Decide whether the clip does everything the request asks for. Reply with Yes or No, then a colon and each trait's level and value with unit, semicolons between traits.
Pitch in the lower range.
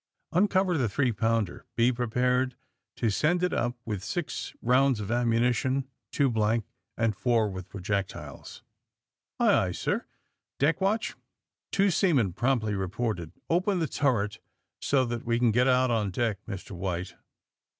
Yes: low, 120 Hz